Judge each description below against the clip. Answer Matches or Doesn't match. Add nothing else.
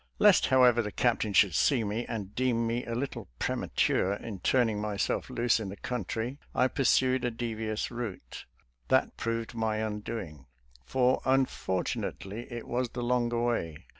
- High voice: Doesn't match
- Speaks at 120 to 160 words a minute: Matches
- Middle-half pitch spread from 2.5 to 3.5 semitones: Matches